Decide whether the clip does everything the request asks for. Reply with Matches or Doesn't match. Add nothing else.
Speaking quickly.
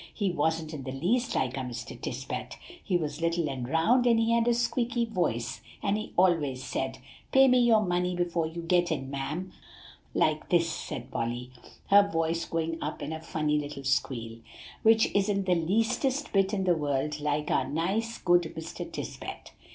Doesn't match